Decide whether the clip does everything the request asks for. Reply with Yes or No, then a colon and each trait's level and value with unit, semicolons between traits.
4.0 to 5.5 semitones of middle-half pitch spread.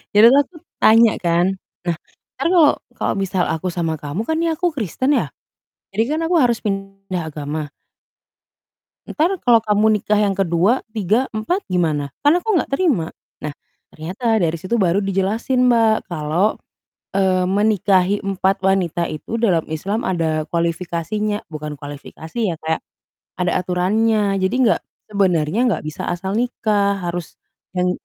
Yes: average, 4.7 semitones